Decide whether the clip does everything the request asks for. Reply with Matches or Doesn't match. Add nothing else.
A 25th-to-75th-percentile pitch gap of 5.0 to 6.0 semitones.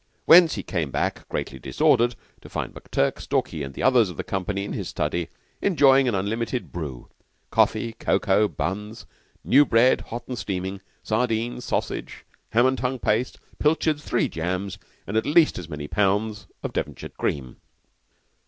Matches